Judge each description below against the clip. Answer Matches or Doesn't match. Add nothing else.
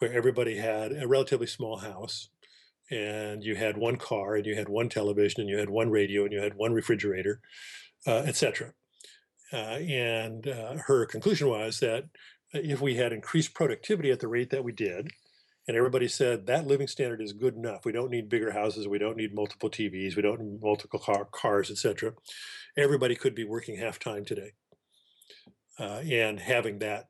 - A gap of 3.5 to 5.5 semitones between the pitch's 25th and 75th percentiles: Doesn't match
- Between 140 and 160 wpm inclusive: Doesn't match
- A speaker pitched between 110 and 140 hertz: Matches